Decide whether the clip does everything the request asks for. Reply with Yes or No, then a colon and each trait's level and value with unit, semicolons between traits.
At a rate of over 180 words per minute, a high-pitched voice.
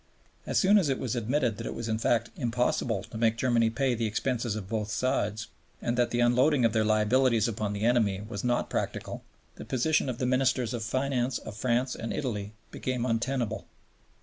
No: average, 200 wpm; low, 120 Hz